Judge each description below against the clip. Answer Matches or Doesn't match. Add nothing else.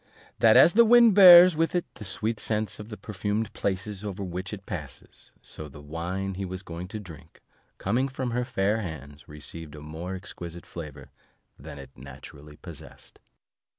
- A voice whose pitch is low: Matches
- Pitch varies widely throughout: Matches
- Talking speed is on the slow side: Doesn't match